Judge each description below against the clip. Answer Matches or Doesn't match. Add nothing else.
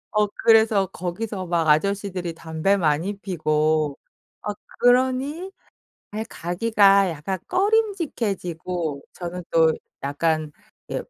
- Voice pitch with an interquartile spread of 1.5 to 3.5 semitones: Doesn't match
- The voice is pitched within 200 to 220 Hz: Doesn't match